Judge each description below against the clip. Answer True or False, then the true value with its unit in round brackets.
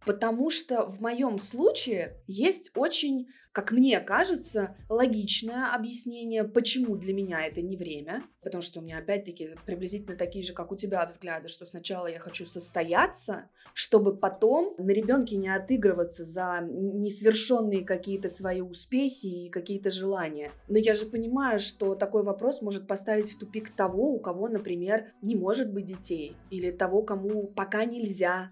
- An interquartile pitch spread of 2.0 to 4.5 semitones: True (3.7 semitones)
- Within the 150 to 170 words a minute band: True (155 wpm)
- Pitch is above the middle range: True (200 Hz)